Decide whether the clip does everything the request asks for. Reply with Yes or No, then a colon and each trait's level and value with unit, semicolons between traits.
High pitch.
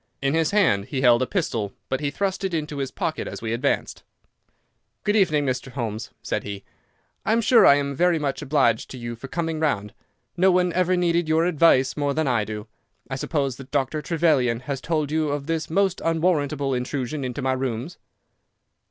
No: medium, 145 Hz